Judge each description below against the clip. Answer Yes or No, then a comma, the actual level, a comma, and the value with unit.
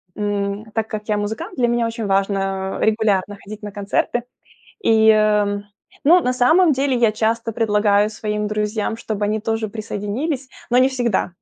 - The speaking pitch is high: Yes, high, 215 Hz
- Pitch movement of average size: No, narrow, 2.2 semitones